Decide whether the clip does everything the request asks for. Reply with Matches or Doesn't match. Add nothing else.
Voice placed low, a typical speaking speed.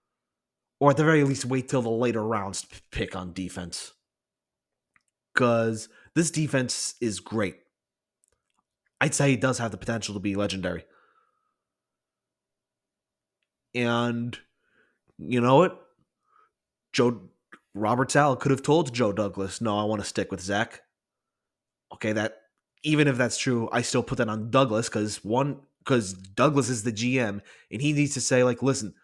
Matches